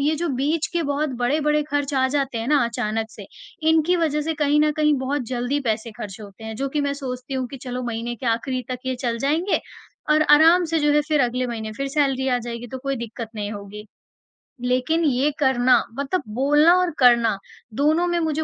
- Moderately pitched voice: No, very high, 270 Hz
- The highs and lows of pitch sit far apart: No, average, 3.8 semitones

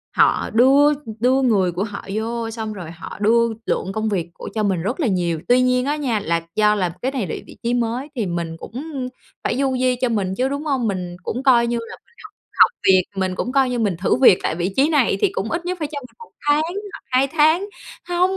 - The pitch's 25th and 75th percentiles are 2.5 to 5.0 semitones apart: No, wide, 5.5 semitones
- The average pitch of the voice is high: Yes, high, 235 Hz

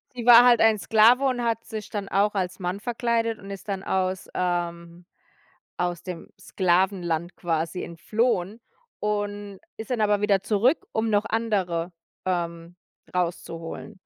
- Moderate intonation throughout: Yes, average, 4.0 semitones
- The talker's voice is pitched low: No, high, 195 Hz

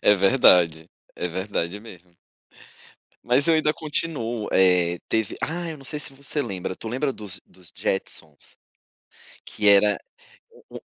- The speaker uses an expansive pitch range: Yes, wide, 7.2 semitones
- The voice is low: Yes, low, 105 Hz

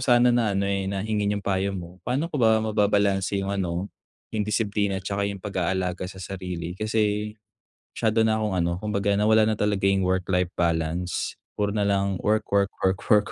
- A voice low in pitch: Yes, low, 100 Hz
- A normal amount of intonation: No, narrow, 2.1 semitones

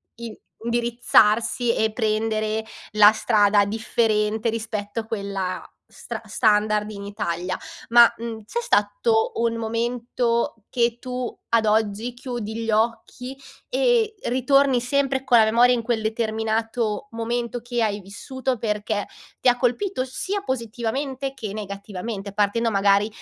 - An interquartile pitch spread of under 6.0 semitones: Yes, narrow, 2.5 semitones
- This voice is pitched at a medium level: No, high, 230 Hz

